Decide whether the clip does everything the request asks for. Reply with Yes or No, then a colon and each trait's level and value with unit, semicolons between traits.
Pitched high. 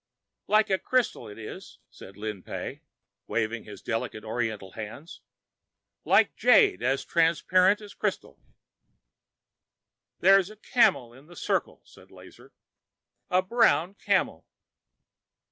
No: medium, 145 Hz